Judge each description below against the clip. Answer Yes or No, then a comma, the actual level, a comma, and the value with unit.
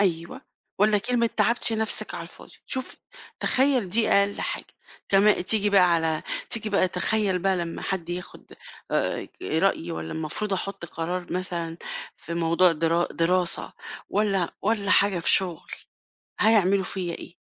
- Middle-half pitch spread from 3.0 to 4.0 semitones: Yes, average, 3.5 semitones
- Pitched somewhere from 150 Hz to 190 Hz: Yes, medium, 185 Hz